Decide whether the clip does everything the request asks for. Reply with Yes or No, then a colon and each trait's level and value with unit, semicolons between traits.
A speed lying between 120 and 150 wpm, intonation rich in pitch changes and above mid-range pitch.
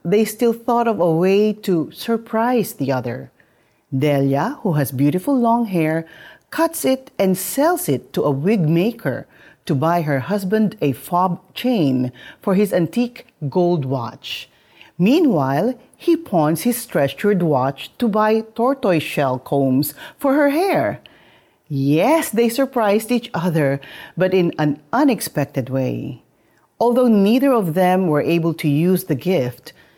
No: average, 140 wpm; wide, 8.2 semitones; medium, 180 Hz